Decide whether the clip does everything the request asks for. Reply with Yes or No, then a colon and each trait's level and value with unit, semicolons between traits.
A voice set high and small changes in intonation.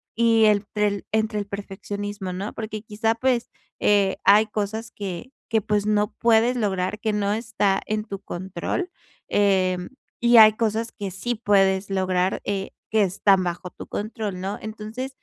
Yes: high, 210 Hz; narrow, 2.2 semitones